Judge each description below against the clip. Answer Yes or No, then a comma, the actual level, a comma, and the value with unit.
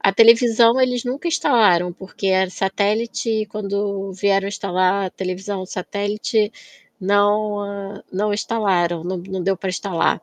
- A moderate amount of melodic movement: No, narrow, 2.1 semitones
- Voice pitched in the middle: No, high, 200 Hz